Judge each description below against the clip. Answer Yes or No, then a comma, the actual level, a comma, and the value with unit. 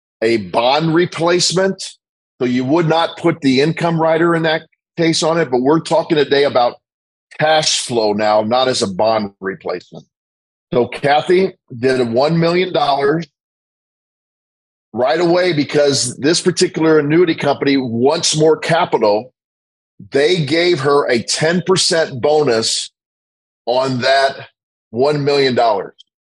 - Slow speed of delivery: Yes, slow, 125 wpm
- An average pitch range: Yes, average, 5.0 semitones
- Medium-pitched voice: Yes, medium, 145 Hz